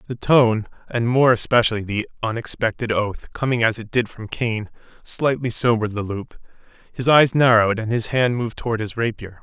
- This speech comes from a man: Yes, male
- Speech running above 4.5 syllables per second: Yes, 5.3 syllables/s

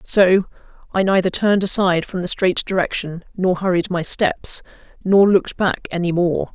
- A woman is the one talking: Yes, female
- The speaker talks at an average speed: Yes, average, 165 wpm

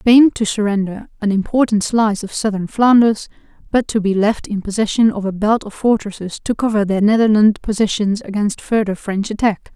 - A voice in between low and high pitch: No, high, 210 Hz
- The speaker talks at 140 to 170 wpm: No, average, 180 wpm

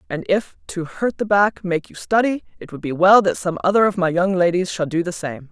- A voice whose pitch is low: No, medium, 185 Hz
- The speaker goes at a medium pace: No, fast, 260 wpm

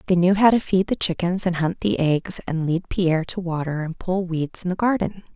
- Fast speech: Yes, fast, 245 wpm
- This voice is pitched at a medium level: Yes, medium, 180 Hz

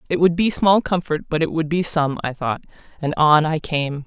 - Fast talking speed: Yes, fast, 235 wpm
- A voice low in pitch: No, medium, 160 Hz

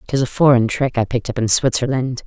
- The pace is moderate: No, fast, 240 wpm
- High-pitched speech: No, low, 125 Hz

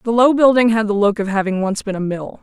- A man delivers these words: No, female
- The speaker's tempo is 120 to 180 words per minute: No, fast, 295 wpm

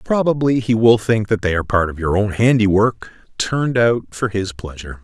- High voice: No, low, 105 Hz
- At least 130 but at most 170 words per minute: No, fast, 205 wpm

